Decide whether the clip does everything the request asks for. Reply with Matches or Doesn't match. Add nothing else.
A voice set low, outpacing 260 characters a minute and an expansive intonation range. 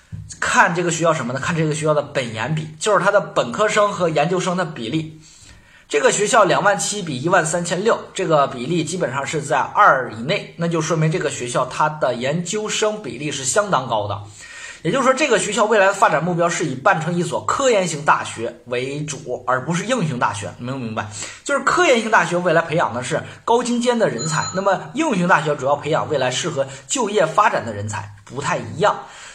Doesn't match